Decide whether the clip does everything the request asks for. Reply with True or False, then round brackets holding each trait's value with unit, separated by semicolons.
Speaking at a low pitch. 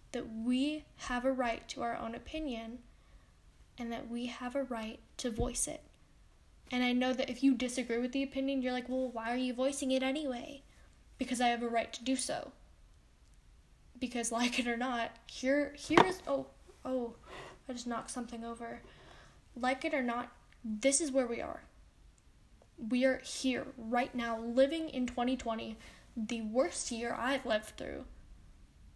False (250 Hz)